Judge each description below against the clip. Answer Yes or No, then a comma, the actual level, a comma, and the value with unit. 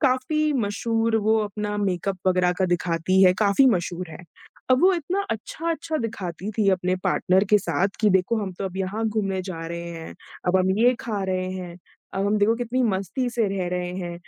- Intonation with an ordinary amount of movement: Yes, average, 3.7 semitones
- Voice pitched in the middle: No, high, 195 Hz